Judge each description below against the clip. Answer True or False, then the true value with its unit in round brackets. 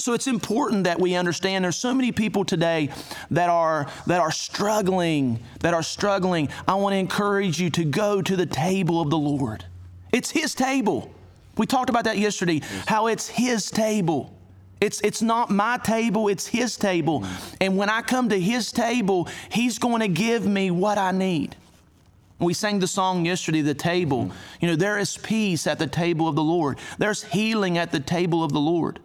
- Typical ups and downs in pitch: True (4.7 semitones)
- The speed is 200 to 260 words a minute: False (190 wpm)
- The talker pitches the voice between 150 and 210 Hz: True (185 Hz)